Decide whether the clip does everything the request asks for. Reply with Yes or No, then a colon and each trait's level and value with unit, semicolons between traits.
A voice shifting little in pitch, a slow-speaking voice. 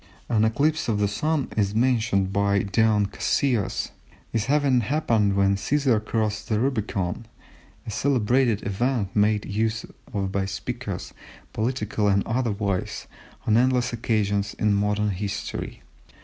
No: average, 3.2 semitones; slow, 130 wpm